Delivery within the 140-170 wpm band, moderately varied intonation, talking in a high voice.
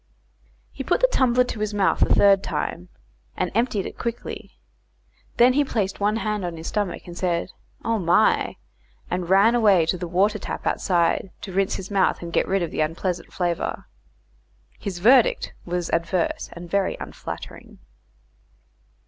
Yes: average, 160 wpm; average, 3.4 semitones; high, 195 Hz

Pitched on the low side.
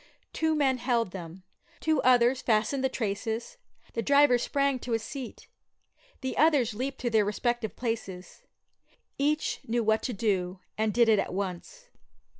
No: high, 240 Hz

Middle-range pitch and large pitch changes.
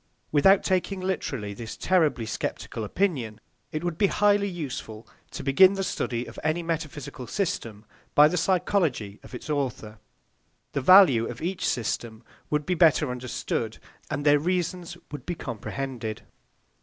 Yes: medium, 150 Hz; wide, 7.1 semitones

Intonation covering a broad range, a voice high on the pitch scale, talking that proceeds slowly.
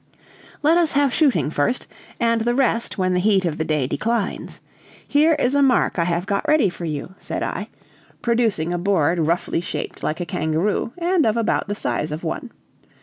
No: wide, 6.6 semitones; high, 200 Hz; average, 195 wpm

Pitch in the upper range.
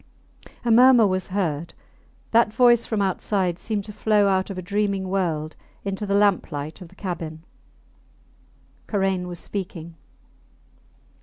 Yes: high, 195 Hz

